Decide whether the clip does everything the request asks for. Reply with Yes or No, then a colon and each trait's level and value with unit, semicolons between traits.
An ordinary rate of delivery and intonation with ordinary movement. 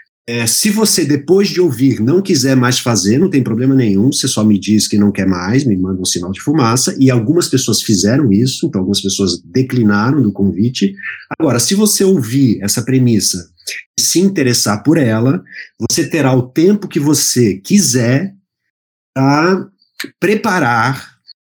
No: average, 165 wpm; wide, 7.0 semitones